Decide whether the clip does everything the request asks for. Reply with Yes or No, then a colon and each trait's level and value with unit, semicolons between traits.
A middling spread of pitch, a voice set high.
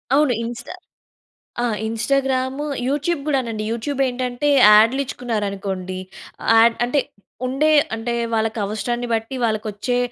Yes: average, 3.2 semitones; high, 240 Hz